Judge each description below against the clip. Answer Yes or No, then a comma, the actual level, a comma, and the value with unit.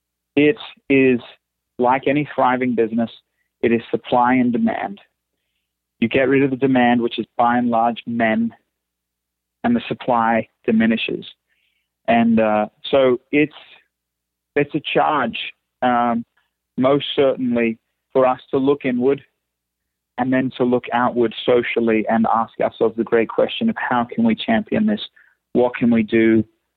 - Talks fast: No, average, 145 wpm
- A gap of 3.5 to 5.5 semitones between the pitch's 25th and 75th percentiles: No, average, 2.8 semitones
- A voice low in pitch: Yes, low, 120 Hz